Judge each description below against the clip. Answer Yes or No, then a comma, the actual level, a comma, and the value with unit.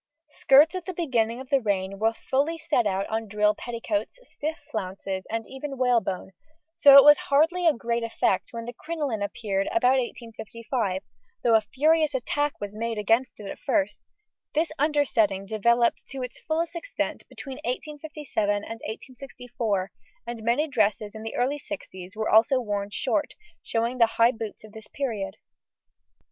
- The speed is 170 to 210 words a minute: No, average, 160 wpm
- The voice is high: Yes, high, 235 Hz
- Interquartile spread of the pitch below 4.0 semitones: No, average, 4.8 semitones